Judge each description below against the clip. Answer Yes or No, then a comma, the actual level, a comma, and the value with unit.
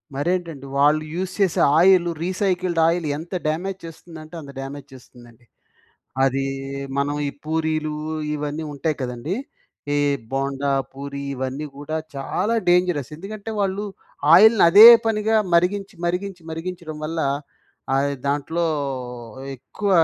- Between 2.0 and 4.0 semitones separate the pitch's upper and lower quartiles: No, average, 4.5 semitones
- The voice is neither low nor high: Yes, medium, 160 Hz